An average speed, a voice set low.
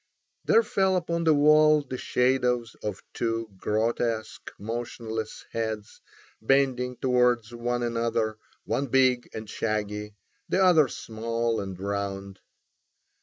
No: slow, 115 wpm; low, 115 Hz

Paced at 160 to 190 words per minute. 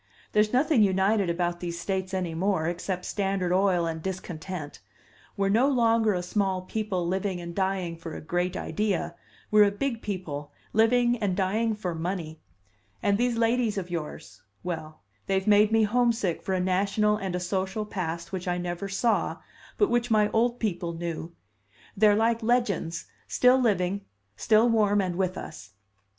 Yes: average, 165 wpm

